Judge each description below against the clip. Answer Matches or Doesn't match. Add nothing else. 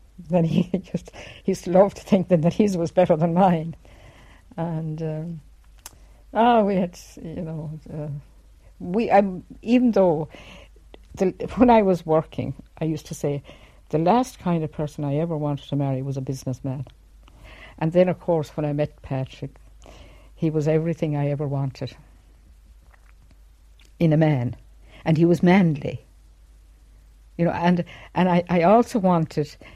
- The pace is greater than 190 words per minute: Doesn't match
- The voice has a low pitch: Doesn't match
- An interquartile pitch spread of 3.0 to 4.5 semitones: Doesn't match